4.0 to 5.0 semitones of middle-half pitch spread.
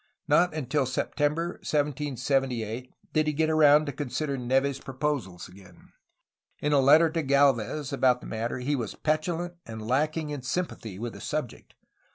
No: average, 3.5 semitones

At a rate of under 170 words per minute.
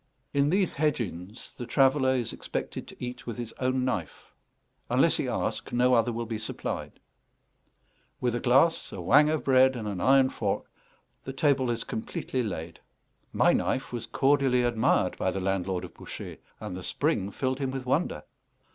No: average, 175 wpm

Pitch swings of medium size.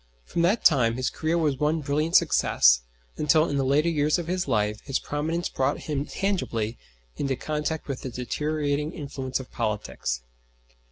Yes: average, 3.4 semitones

